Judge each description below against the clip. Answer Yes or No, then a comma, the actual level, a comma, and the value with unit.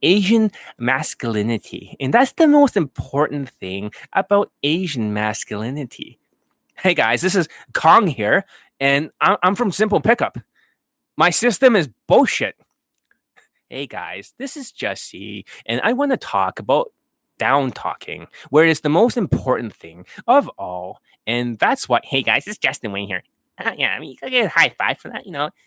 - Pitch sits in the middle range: Yes, medium, 150 Hz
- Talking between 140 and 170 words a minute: Yes, average, 160 wpm